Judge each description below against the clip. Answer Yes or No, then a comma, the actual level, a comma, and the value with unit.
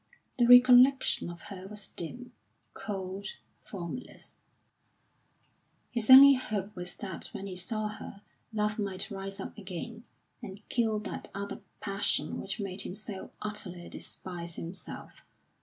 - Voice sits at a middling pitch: No, high, 200 Hz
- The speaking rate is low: Yes, slow, 130 wpm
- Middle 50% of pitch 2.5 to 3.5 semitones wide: Yes, average, 2.8 semitones